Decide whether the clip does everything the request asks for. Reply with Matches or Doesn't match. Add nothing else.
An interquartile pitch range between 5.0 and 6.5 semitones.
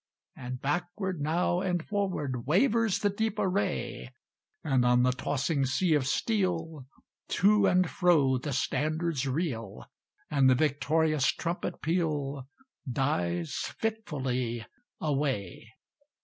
Matches